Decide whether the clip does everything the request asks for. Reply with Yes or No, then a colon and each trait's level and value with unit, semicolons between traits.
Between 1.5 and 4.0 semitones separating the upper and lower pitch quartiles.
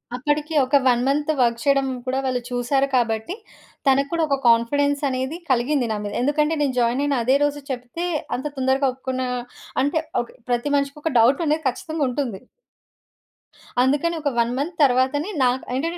Yes: average, 2.8 semitones